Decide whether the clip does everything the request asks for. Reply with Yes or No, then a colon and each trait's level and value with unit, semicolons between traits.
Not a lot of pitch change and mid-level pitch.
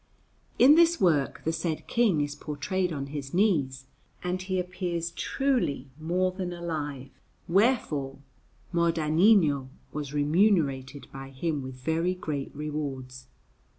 No: average, 4.5 semitones; medium, 160 Hz